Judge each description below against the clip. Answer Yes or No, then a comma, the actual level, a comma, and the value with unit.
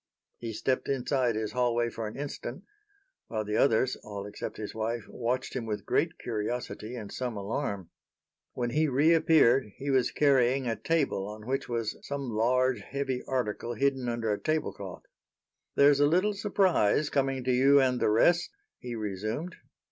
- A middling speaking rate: Yes, average, 165 wpm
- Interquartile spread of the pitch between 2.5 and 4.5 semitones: Yes, average, 4.1 semitones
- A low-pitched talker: Yes, low, 125 Hz